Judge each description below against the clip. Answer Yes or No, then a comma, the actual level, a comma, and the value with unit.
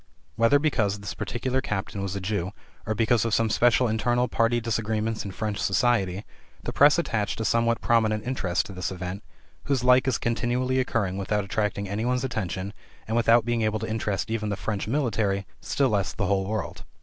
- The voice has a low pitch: Yes, low, 110 Hz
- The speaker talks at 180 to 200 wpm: Yes, average, 190 wpm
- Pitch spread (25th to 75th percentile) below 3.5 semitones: Yes, average, 3.0 semitones